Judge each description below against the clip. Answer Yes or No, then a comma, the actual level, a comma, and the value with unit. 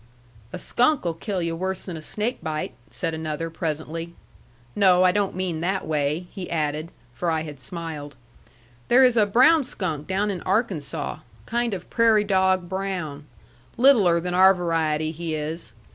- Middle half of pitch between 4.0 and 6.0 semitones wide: No, average, 3.6 semitones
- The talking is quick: No, average, 160 wpm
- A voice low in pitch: No, medium, 175 Hz